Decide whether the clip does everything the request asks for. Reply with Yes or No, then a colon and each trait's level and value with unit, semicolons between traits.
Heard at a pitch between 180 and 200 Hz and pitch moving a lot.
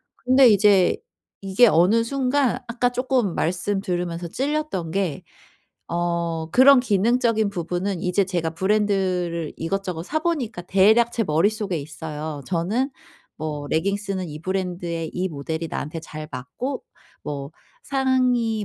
Yes: high, 190 Hz; wide, 5.7 semitones